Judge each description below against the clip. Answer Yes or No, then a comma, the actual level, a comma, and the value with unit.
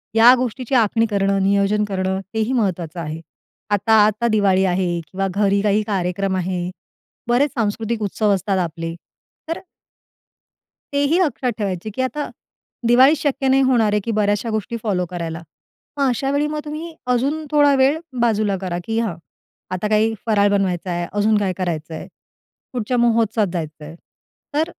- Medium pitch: No, high, 210 Hz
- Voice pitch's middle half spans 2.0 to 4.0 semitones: No, average, 4.4 semitones